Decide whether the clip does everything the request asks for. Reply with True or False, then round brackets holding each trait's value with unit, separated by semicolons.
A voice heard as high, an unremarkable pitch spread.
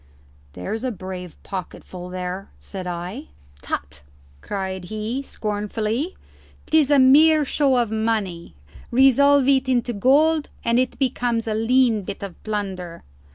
False (220 Hz; 5.7 semitones)